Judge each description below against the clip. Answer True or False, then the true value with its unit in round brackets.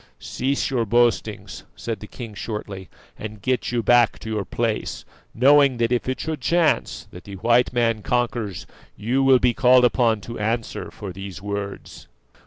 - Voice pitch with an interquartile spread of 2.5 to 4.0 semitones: True (2.8 semitones)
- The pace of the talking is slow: False (170 wpm)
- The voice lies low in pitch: True (115 Hz)